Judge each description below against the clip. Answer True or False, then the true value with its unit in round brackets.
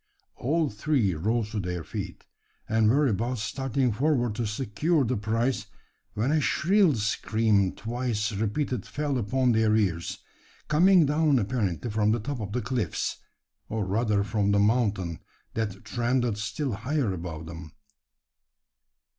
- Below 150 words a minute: True (140 wpm)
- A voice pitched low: True (115 Hz)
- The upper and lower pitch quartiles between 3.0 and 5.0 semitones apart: True (4.3 semitones)